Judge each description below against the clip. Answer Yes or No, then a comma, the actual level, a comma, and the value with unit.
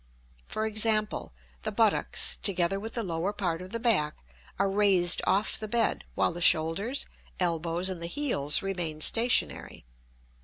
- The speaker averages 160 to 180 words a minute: No, average, 150 wpm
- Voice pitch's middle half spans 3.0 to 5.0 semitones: Yes, average, 4.3 semitones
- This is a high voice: Yes, high, 195 Hz